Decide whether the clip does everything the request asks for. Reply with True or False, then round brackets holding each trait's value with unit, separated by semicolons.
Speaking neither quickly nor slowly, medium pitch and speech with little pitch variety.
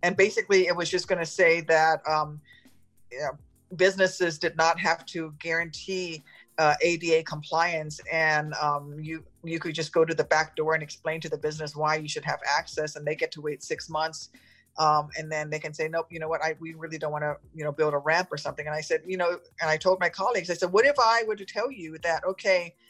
False (245 wpm; 160 Hz; 2.2 semitones)